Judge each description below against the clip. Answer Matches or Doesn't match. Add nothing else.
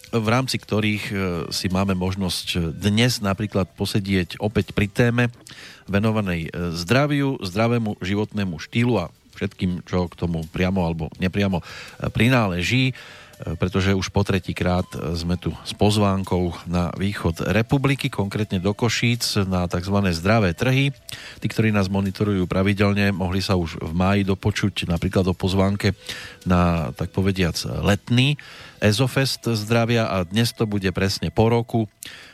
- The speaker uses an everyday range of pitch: Matches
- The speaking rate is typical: Matches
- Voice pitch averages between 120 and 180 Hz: Doesn't match